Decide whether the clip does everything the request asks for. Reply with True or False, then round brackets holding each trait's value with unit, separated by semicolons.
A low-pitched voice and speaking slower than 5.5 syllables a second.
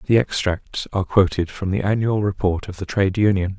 False (100 Hz; 5.7 syllables/s)